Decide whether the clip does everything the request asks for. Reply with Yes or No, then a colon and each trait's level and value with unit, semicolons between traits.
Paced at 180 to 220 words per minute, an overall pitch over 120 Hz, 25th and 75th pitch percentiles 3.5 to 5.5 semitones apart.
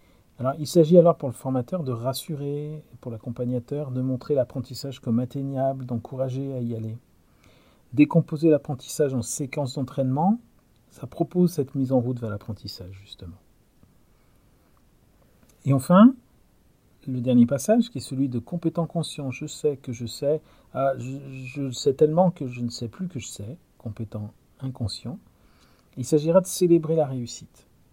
No: average, 150 wpm; low, 135 Hz; average, 3.9 semitones